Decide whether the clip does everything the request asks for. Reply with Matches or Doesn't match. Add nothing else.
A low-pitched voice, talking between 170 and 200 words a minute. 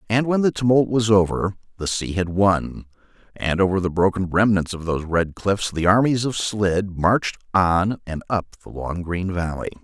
Matches